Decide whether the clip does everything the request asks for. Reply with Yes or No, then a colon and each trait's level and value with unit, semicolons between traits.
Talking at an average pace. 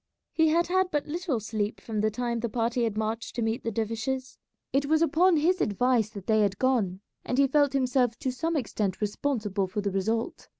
No: fast, 210 wpm